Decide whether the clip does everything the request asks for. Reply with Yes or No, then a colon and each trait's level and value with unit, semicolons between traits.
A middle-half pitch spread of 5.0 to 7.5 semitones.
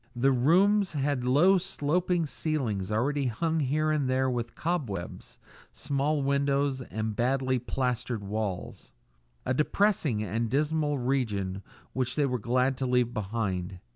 No: average, 4.2 semitones